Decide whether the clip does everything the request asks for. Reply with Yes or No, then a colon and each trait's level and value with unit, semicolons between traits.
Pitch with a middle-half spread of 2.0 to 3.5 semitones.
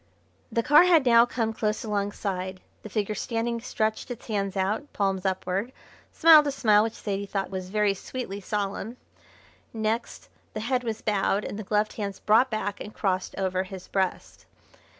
Yes: average, 3.0 semitones